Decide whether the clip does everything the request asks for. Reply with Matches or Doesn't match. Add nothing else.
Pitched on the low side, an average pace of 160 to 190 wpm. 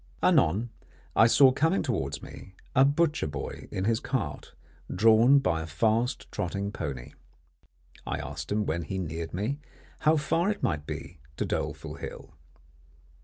Doesn't match